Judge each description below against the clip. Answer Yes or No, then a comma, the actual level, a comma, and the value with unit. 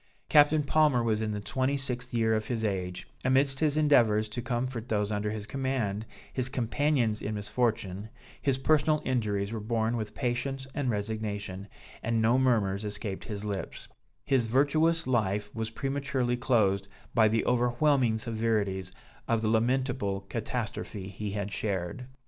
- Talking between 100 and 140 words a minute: No, average, 150 wpm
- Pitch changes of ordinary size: Yes, average, 3.9 semitones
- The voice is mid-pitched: No, low, 115 Hz